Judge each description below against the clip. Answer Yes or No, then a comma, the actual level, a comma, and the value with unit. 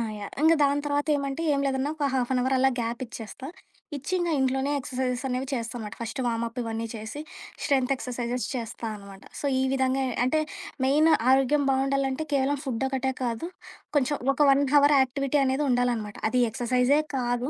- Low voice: No, very high, 260 Hz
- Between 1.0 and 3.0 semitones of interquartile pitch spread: Yes, narrow, 2.4 semitones